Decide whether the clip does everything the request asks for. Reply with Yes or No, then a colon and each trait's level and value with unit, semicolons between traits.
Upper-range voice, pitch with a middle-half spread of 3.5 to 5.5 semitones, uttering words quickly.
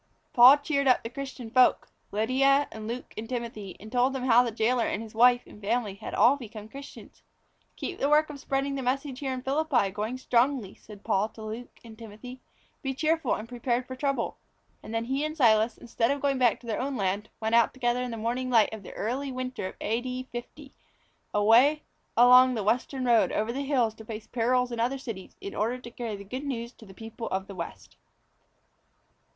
No: high, 245 Hz; average, 3.1 semitones; fast, 215 wpm